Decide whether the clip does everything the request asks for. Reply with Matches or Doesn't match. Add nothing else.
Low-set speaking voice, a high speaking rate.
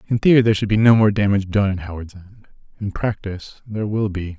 Matches